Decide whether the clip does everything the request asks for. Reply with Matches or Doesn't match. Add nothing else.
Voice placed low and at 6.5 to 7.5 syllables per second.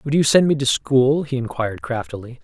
Doesn't match